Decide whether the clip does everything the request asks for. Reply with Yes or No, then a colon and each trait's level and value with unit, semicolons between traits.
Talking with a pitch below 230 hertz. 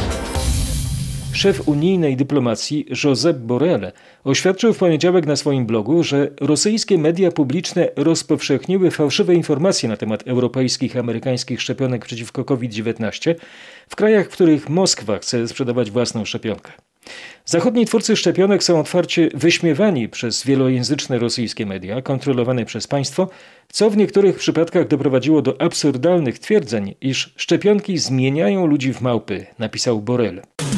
Yes: medium, 140 Hz